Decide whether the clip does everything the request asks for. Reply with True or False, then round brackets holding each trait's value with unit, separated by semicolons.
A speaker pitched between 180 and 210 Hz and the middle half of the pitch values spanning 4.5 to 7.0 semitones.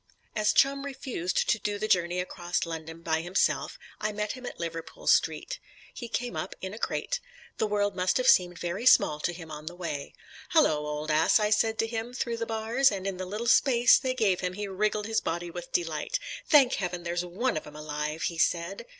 True (190 Hz; 4.8 semitones)